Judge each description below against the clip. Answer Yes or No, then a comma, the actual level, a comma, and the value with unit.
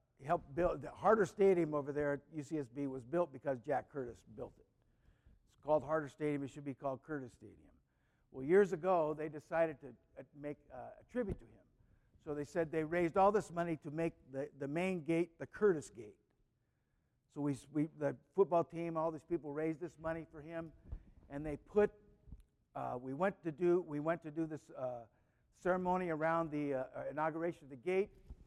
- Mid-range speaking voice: Yes, medium, 155 Hz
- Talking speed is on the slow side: No, average, 195 wpm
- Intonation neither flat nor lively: Yes, average, 3.6 semitones